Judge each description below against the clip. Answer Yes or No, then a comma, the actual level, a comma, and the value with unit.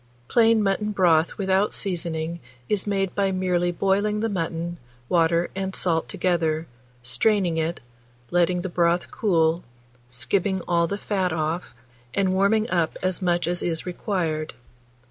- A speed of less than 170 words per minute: Yes, average, 140 wpm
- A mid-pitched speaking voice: Yes, medium, 180 Hz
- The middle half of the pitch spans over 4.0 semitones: No, average, 2.7 semitones